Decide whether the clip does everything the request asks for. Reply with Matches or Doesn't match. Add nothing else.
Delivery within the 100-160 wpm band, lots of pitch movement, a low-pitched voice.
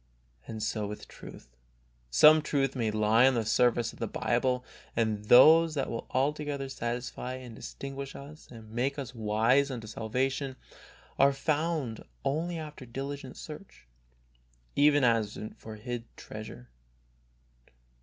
Doesn't match